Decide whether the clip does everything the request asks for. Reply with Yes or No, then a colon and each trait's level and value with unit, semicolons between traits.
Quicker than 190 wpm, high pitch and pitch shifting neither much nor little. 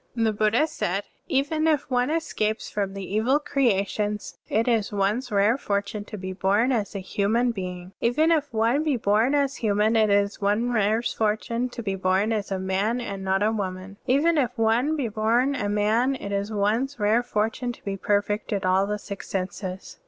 Yes: average, 200 wpm; high, 215 Hz; average, 3.4 semitones